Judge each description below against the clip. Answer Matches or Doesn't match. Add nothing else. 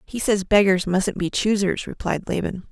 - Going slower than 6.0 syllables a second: Matches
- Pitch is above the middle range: Matches